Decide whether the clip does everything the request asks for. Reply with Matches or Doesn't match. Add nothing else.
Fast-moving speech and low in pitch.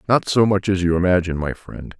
Matches